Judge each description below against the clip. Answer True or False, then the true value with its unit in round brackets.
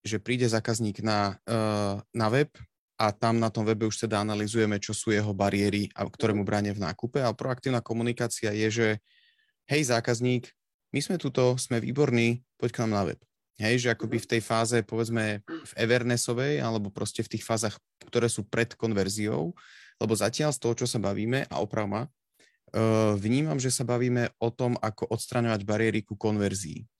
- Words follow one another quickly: True (180 wpm)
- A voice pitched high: False (115 Hz)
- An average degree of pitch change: False (2.2 semitones)